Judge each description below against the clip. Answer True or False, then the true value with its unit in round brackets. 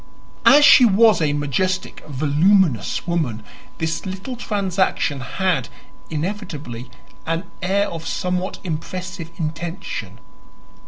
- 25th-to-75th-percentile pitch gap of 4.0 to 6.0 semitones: True (4.3 semitones)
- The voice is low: False (180 Hz)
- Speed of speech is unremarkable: False (100 wpm)